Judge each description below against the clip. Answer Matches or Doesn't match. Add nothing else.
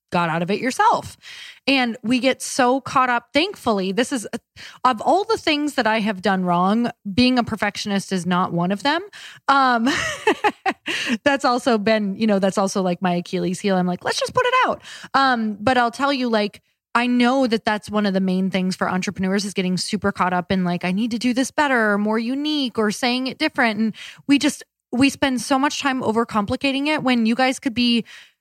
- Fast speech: Matches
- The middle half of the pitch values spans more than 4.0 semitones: Matches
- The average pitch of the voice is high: Matches